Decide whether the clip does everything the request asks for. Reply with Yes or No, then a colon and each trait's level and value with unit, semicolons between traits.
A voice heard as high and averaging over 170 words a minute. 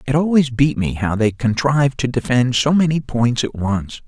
No: low, 130 Hz; fast, 205 wpm